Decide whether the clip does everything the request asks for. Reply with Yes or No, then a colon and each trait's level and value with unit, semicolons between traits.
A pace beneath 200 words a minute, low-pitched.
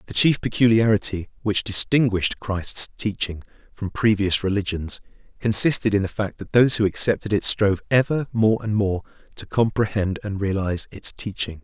Yes: average, 155 wpm; low, 105 Hz